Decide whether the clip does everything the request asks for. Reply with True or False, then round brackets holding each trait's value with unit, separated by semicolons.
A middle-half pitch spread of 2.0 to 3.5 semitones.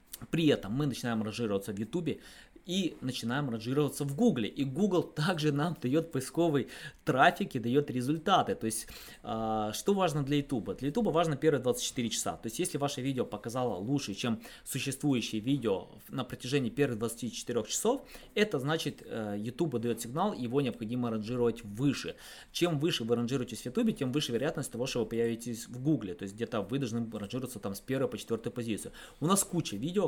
False (4.6 semitones)